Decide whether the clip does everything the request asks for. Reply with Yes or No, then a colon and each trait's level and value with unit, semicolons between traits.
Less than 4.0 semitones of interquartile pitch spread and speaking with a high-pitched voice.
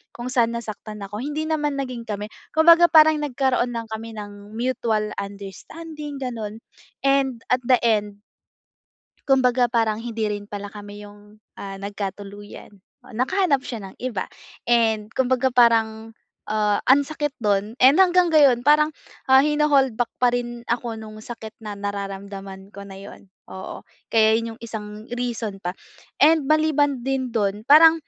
No: average, 4.4 semitones; high, 230 Hz